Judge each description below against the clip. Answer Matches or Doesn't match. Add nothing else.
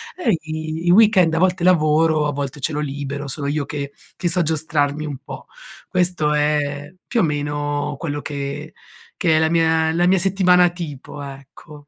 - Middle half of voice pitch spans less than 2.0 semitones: Doesn't match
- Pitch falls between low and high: Matches